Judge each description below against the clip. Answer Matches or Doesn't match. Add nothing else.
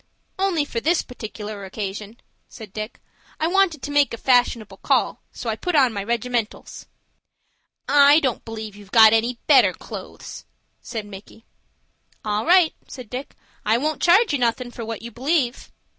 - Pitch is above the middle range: Matches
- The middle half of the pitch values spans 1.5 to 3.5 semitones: Doesn't match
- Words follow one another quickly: Doesn't match